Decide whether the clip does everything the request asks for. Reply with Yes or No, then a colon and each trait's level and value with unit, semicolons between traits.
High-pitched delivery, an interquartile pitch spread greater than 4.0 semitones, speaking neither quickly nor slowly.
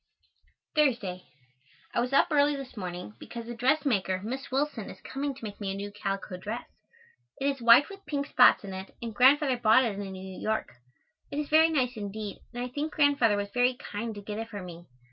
No: high, 235 Hz; average, 5.2 semitones; fast, 210 wpm